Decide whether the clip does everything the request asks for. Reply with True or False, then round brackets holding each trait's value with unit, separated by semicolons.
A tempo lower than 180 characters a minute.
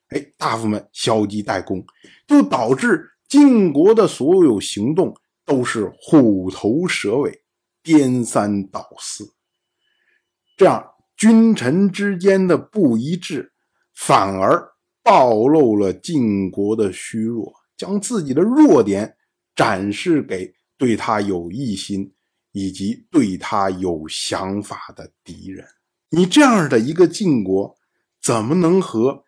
True (170 characters per minute)